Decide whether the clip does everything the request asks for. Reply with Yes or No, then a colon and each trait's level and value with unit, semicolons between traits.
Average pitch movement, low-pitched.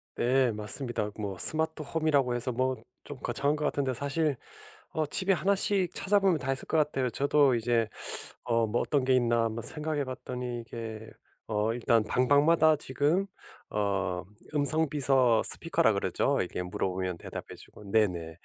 Yes: average, 4.9 semitones; low, 130 Hz